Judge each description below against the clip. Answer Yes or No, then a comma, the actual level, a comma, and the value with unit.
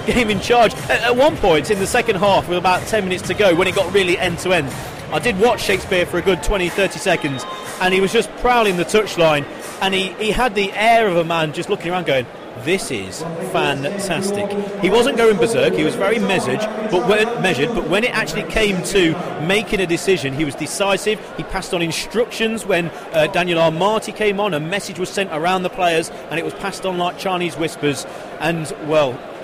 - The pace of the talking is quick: Yes, fast, 215 wpm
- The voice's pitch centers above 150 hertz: Yes, high, 190 Hz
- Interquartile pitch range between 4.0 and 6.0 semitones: No, average, 3.6 semitones